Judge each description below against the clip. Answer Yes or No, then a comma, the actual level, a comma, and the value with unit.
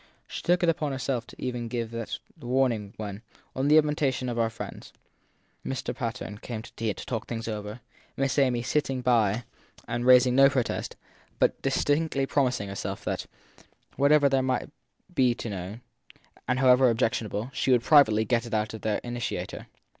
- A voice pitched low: Yes, low, 125 Hz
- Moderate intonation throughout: Yes, average, 3.0 semitones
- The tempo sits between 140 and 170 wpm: No, average, 180 wpm